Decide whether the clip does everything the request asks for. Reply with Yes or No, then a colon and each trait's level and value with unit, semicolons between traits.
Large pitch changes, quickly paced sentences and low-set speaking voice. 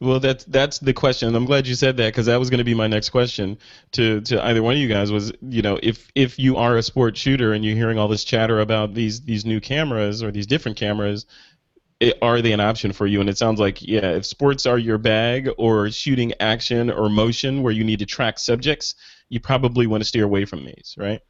No: average, 2.7 semitones; fast, 250 wpm; low, 115 Hz